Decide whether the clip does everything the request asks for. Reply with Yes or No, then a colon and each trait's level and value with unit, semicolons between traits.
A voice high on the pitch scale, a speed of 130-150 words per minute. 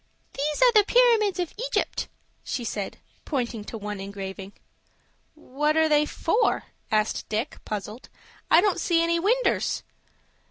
Yes: very high, 300 Hz; slow, 135 wpm